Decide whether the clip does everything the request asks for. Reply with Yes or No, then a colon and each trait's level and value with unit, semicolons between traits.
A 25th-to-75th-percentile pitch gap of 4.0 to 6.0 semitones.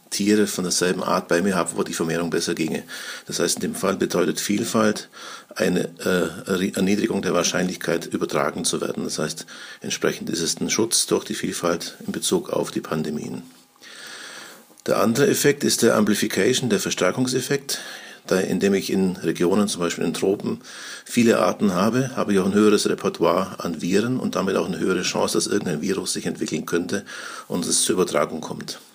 No: average, 3.3 semitones